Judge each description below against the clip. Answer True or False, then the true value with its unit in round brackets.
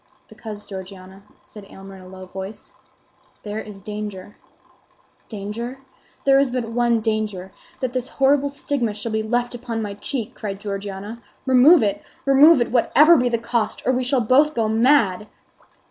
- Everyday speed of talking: True (160 wpm)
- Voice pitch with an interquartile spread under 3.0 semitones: False (3.7 semitones)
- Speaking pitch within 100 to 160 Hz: False (225 Hz)